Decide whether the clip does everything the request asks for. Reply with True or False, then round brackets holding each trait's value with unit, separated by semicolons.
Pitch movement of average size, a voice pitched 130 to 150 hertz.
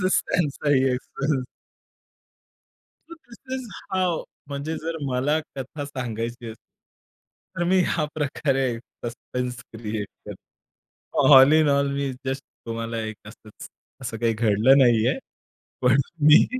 True (4.2 semitones; 135 Hz)